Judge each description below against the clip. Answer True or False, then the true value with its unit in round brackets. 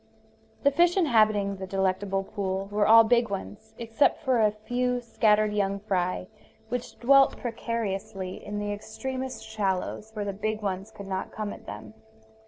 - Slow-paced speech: False (160 wpm)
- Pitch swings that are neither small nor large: True (3.2 semitones)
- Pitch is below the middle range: False (210 Hz)